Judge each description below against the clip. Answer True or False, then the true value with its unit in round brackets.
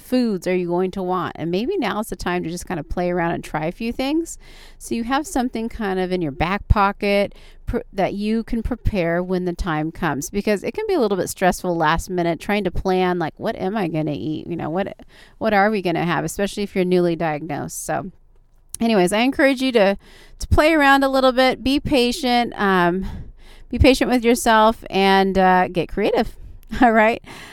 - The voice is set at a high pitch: True (195 Hz)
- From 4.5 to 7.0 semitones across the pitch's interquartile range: True (4.8 semitones)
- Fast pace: True (220 wpm)